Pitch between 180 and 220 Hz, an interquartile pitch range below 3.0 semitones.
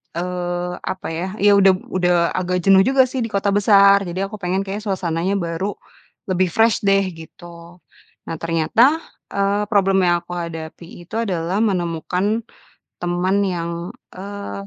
Yes: medium, 185 Hz; narrow, 2.5 semitones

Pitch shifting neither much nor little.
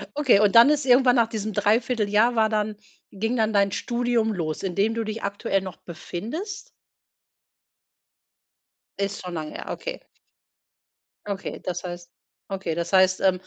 Yes: average, 3.6 semitones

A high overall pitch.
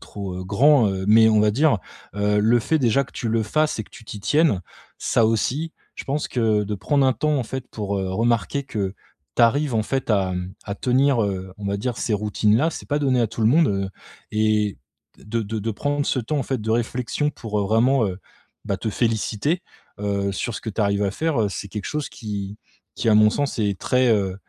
No: low, 110 Hz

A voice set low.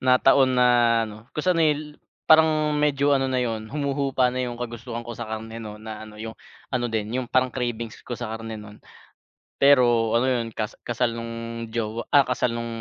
Yes: low, 120 Hz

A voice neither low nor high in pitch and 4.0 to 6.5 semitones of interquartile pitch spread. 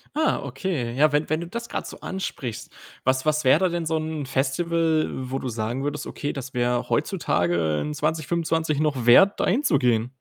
Yes: medium, 145 Hz; average, 4.3 semitones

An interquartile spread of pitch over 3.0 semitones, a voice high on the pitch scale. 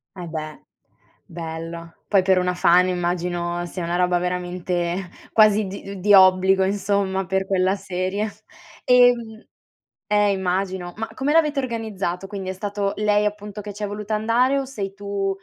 No: average, 2.7 semitones; high, 195 Hz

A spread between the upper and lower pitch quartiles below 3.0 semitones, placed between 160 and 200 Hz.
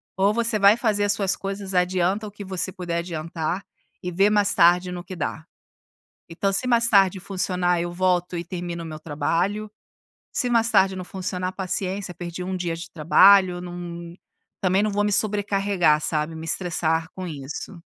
Yes: narrow, 2.6 semitones; medium, 185 Hz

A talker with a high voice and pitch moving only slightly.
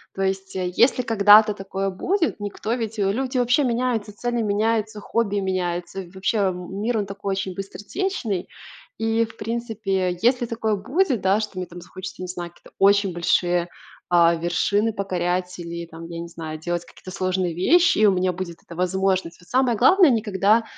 No: high, 195 Hz; average, 3.8 semitones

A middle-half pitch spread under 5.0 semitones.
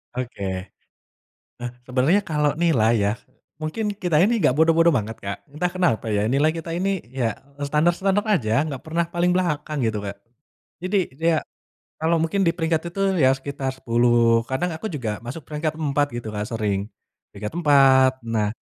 No: wide, 5.5 semitones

